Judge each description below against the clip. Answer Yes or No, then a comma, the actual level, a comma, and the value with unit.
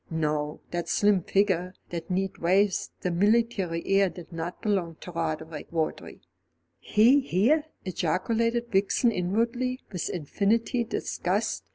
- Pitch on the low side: No, high, 190 Hz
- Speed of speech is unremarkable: No, slow, 125 wpm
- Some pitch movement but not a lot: Yes, average, 4.9 semitones